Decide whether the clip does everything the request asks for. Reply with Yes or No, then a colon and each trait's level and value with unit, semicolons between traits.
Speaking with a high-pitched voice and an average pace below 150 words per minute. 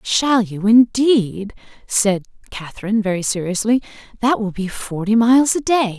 Yes: high, 215 Hz; average, 140 wpm